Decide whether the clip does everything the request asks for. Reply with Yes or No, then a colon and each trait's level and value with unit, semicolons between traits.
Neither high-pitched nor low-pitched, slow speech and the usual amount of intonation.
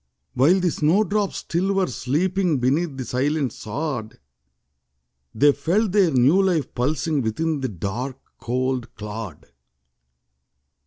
No: medium, 145 Hz; slow, 120 wpm; wide, 5.8 semitones